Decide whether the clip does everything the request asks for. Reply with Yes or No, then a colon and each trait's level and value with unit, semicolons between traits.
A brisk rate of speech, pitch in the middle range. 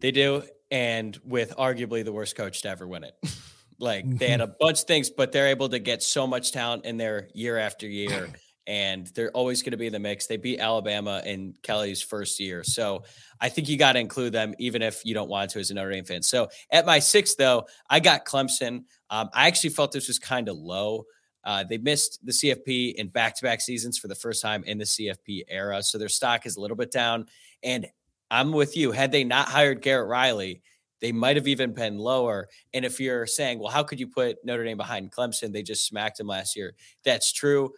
No: fast, 235 wpm; low, 115 Hz